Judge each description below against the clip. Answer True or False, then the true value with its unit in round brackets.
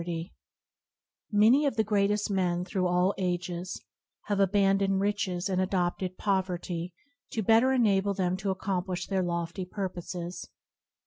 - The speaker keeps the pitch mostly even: True (2.2 semitones)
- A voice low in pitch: False (190 Hz)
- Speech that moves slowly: True (125 wpm)